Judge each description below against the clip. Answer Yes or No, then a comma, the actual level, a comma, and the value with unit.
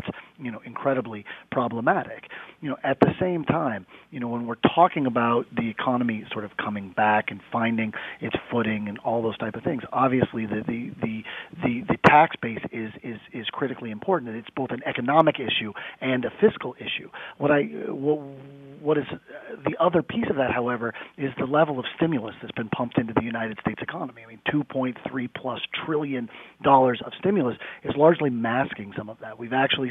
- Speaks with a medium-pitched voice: No, low, 130 Hz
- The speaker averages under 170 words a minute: No, average, 195 wpm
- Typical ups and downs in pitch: Yes, average, 4.1 semitones